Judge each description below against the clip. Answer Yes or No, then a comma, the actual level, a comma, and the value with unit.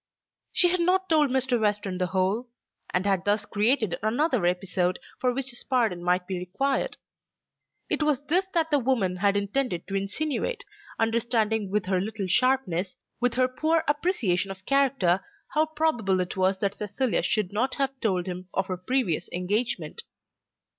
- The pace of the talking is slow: No, average, 165 wpm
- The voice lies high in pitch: Yes, high, 220 Hz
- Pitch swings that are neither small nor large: No, wide, 6.1 semitones